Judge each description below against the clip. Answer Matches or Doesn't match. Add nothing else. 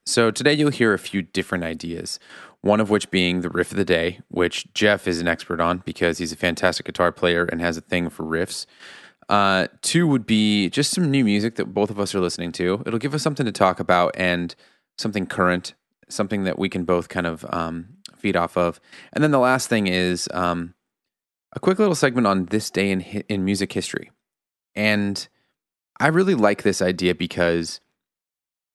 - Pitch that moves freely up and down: Doesn't match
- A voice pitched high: Doesn't match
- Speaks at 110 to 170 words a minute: Doesn't match